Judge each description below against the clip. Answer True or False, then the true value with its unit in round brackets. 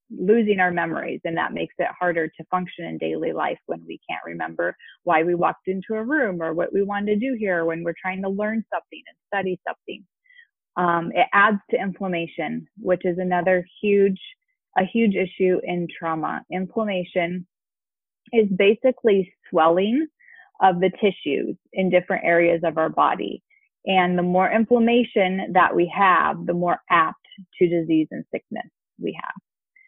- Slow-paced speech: False (165 wpm)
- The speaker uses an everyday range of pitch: True (3.2 semitones)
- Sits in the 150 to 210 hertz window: True (185 Hz)